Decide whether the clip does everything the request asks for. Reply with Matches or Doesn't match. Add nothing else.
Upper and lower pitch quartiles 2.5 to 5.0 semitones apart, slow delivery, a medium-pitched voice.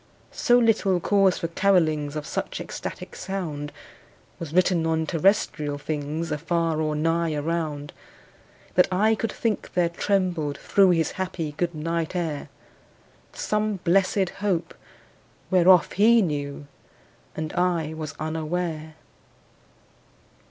Matches